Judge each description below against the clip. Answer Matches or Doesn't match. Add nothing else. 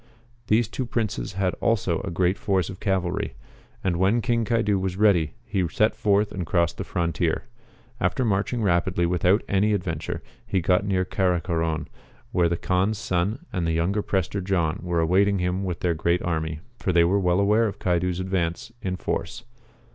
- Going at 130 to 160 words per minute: Doesn't match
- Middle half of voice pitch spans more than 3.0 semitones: Doesn't match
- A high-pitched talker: Doesn't match